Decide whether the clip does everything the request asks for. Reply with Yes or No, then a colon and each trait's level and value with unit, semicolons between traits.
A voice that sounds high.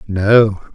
No: low, 105 Hz